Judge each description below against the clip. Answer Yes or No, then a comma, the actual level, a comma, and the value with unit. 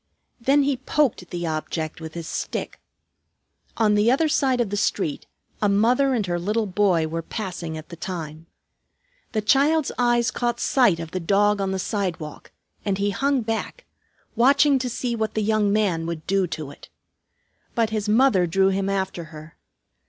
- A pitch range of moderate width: No, wide, 5.7 semitones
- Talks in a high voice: Yes, high, 205 Hz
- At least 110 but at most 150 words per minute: No, average, 175 wpm